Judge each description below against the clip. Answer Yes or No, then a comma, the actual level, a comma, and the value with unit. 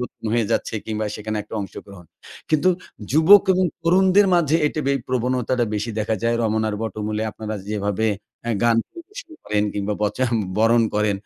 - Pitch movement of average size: No, wide, 5.8 semitones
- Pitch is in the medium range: No, low, 115 Hz